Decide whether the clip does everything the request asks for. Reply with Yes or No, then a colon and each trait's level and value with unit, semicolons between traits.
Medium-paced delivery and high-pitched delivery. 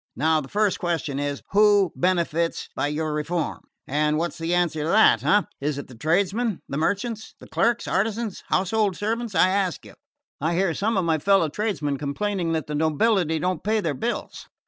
No: average, 190 wpm; medium, 175 Hz